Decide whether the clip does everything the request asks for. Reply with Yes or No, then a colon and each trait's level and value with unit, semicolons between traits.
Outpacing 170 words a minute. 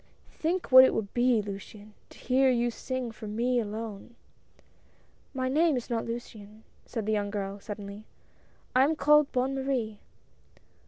No: average, 160 wpm